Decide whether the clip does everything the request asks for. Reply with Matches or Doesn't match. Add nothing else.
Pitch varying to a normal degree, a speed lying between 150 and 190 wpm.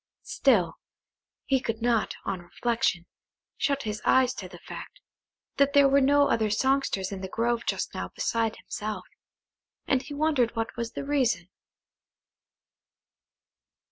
Doesn't match